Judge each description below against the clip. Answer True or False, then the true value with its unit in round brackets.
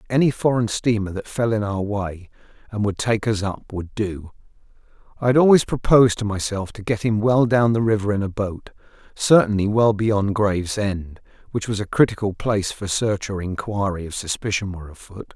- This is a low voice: True (105 Hz)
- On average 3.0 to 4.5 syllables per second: False (5.3 syllables/s)